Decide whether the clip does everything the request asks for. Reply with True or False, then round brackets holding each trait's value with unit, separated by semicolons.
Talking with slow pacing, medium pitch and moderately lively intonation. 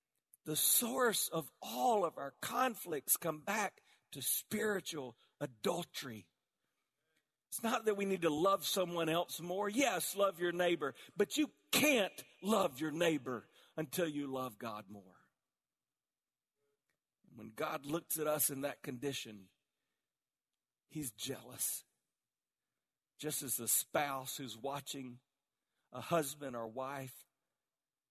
True (120 wpm; 150 Hz; 5.0 semitones)